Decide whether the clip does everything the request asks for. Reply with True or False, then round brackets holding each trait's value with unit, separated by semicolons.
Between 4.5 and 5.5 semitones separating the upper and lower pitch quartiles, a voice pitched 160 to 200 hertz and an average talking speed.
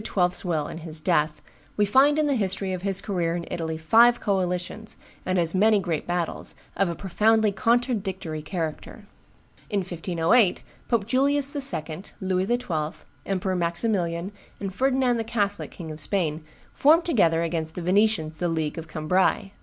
True (4.8 semitones; 185 Hz; 160 wpm)